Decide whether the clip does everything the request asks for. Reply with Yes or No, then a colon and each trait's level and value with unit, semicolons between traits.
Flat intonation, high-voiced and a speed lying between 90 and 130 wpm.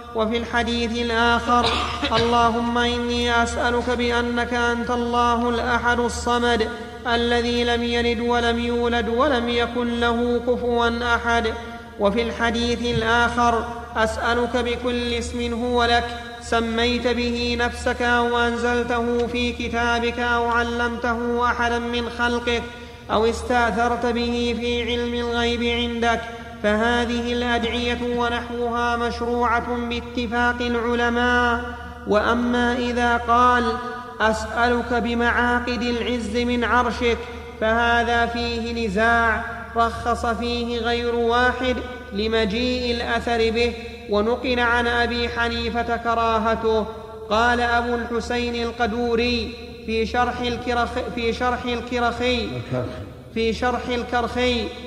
Yes: narrow, 0.4 semitones; high, 235 Hz; average, 100 wpm